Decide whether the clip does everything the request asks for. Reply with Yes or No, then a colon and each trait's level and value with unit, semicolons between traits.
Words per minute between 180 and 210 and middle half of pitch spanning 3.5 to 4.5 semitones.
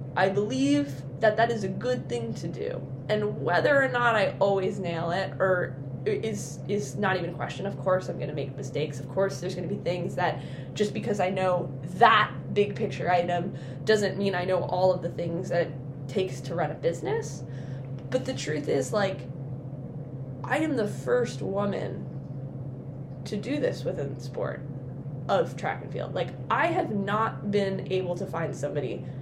No: average, 190 wpm; wide, 5.6 semitones